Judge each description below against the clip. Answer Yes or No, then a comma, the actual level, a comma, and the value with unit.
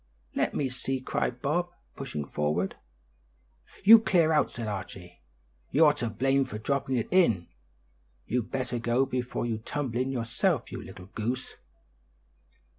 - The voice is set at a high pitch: No, low, 125 Hz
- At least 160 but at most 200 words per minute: No, average, 140 wpm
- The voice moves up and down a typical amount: Yes, average, 3.8 semitones